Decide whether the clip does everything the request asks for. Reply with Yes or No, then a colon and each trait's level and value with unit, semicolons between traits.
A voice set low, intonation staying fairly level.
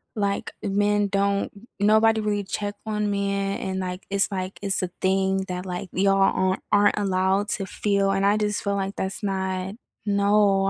No: high, 200 Hz; narrow, 1.3 semitones